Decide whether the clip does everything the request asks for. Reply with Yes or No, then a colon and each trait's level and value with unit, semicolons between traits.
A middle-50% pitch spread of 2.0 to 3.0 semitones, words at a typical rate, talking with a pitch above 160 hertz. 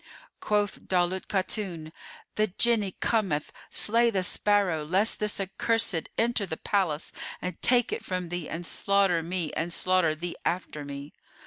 No: average, 3.7 semitones; average, 145 wpm; medium, 185 Hz